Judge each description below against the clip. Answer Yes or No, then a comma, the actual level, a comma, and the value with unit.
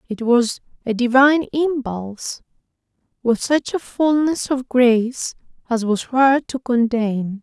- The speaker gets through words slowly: Yes, slow, 130 wpm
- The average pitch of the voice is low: No, very high, 250 Hz